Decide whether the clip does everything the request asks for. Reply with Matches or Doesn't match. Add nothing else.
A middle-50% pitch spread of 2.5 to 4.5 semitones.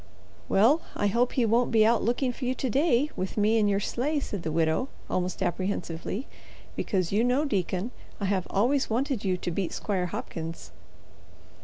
Doesn't match